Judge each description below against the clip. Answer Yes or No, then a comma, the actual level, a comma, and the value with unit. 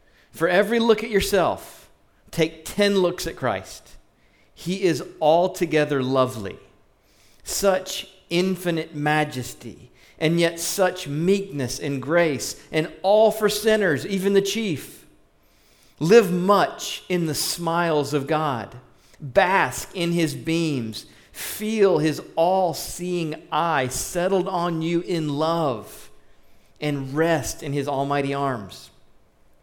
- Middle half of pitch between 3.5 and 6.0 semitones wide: Yes, average, 4.6 semitones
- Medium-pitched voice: Yes, medium, 165 Hz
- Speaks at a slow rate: Yes, slow, 115 wpm